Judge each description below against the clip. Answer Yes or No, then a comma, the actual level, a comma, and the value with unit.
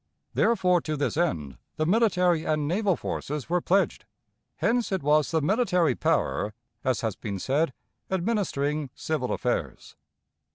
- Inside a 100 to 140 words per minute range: Yes, slow, 135 wpm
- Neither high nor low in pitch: Yes, medium, 160 Hz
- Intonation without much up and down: No, average, 4.8 semitones